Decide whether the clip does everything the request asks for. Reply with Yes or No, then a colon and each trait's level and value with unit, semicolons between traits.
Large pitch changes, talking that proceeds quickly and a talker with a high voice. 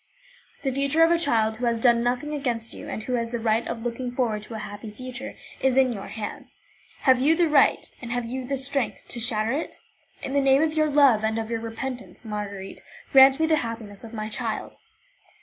No: average, 3.3 semitones; fast, 220 wpm; high, 245 Hz